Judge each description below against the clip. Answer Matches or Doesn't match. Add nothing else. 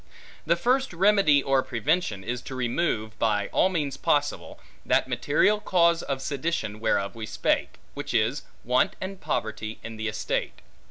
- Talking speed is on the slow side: Doesn't match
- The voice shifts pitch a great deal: Matches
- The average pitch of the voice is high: Doesn't match